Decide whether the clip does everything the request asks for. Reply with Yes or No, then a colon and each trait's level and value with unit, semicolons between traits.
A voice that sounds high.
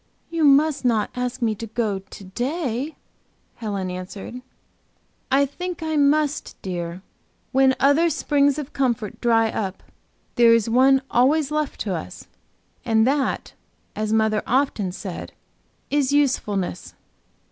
Yes: very high, 250 Hz